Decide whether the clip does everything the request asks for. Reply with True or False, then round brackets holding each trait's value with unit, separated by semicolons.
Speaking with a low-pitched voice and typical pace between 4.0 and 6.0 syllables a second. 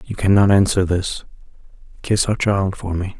True (95 Hz; 4.7 syllables/s)